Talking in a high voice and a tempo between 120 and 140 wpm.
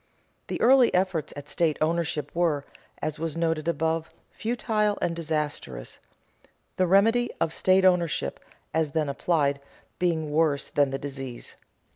No: medium, 160 Hz; slow, 135 wpm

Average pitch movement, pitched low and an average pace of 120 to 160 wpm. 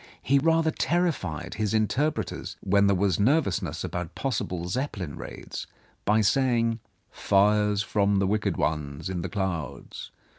Yes: average, 4.8 semitones; low, 100 Hz; slow, 135 wpm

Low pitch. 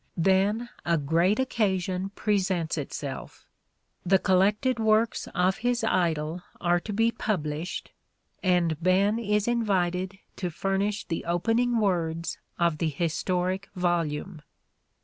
No: medium, 185 Hz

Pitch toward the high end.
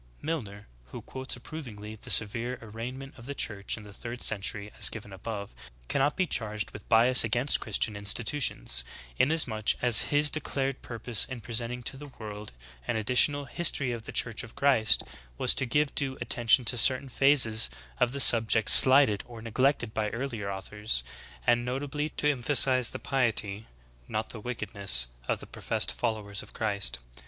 No: low, 115 Hz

